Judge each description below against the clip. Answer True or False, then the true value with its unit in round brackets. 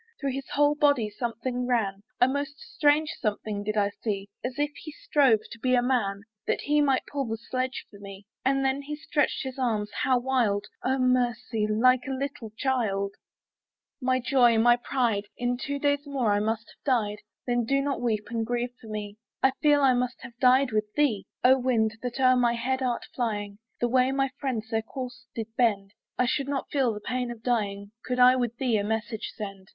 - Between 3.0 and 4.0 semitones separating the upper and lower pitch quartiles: True (3.3 semitones)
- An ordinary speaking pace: False (210 wpm)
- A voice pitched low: False (245 Hz)